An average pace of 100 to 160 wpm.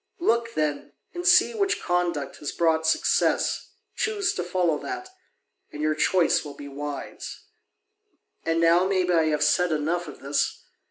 Yes: average, 155 wpm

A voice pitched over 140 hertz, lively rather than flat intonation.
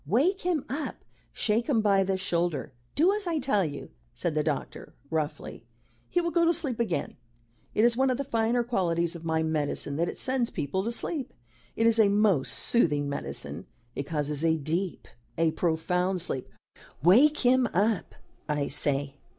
Yes: high, 190 Hz; wide, 7.4 semitones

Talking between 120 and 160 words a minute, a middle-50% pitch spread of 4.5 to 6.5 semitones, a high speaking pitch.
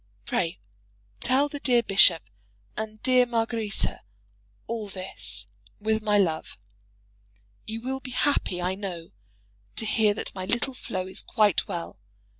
No: slow, 135 wpm; average, 4.1 semitones; high, 215 Hz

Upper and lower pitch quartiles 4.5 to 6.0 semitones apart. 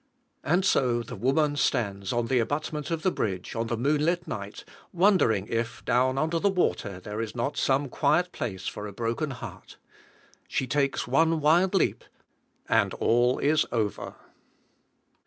Yes: average, 5.3 semitones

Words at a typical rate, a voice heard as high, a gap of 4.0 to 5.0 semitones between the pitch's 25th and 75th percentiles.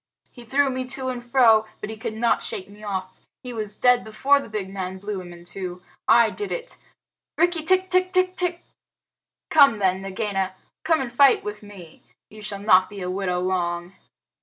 No: average, 190 wpm; high, 215 Hz; wide, 5.6 semitones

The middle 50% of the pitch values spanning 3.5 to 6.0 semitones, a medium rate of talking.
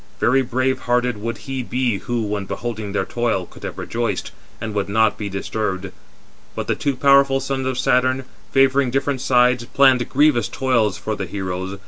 Yes: average, 4.1 semitones; average, 175 wpm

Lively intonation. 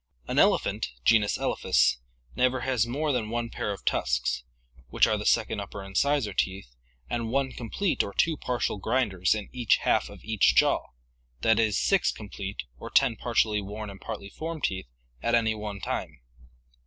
No: average, 3.8 semitones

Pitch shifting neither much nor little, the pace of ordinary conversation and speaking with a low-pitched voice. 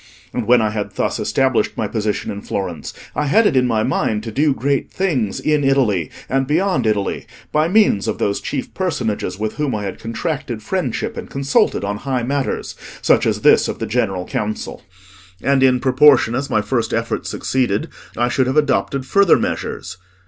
Yes: average, 4.6 semitones; average, 185 wpm; low, 125 Hz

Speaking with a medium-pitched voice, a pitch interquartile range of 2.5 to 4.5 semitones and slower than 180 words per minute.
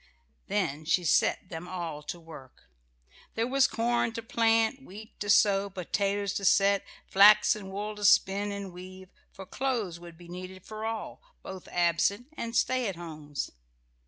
No: high, 195 Hz; average, 3.6 semitones; average, 160 wpm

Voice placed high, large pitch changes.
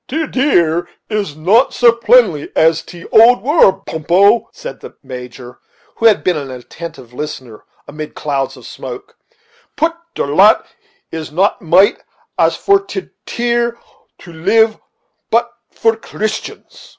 Yes: high, 195 Hz; wide, 7.3 semitones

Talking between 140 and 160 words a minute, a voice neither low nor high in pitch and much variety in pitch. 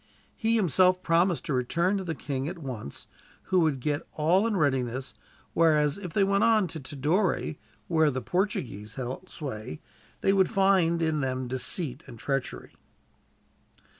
Yes: average, 155 wpm; medium, 160 Hz; wide, 5.9 semitones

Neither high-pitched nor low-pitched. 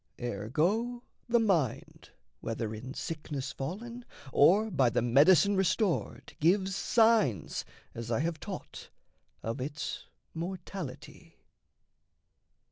Yes: medium, 160 Hz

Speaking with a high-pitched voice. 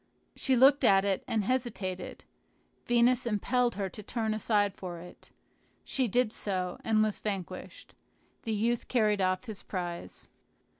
Yes: high, 215 Hz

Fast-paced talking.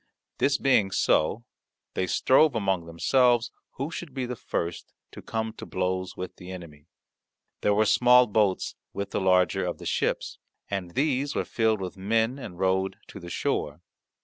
No: average, 170 wpm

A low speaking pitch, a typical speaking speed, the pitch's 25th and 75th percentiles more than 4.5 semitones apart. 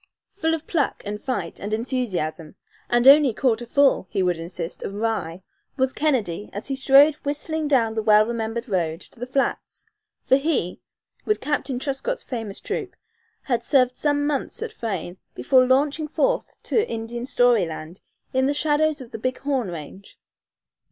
No: high, 245 Hz; average, 165 wpm; wide, 5.6 semitones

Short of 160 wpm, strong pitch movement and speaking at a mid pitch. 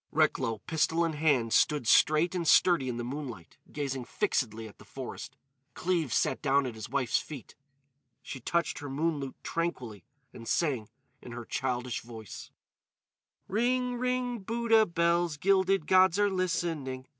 Yes: average, 150 wpm; wide, 6.4 semitones; medium, 150 Hz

